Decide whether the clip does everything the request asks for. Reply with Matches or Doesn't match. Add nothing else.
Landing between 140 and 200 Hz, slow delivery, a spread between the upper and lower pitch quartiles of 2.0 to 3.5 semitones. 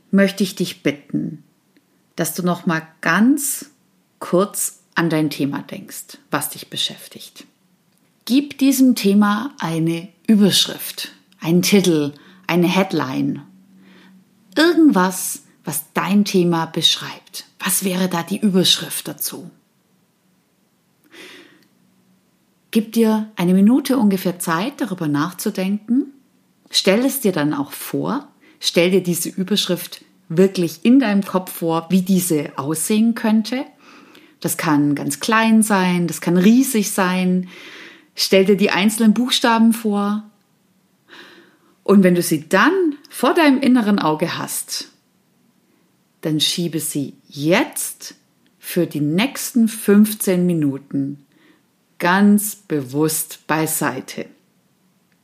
Doesn't match